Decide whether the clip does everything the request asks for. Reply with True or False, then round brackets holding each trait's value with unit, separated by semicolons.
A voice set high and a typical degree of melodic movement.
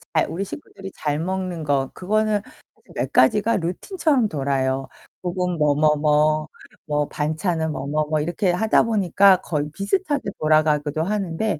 False (165 Hz; 4.8 semitones)